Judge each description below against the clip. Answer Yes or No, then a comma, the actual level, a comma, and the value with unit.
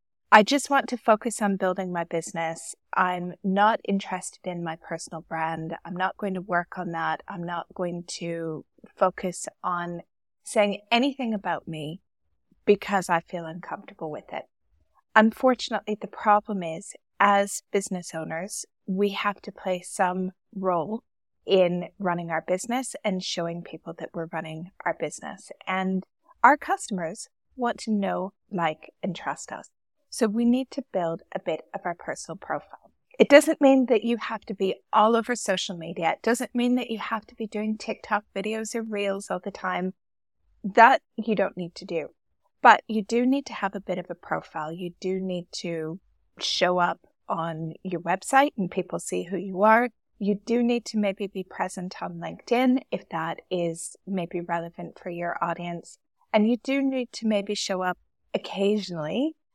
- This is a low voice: No, high, 190 Hz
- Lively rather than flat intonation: No, average, 4.1 semitones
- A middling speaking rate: Yes, average, 170 wpm